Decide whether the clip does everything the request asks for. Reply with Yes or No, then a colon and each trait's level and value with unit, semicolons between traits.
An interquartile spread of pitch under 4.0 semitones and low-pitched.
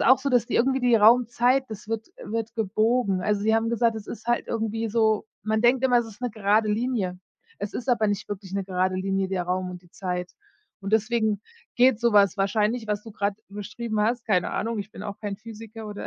No: narrow, 2.6 semitones; high, 215 Hz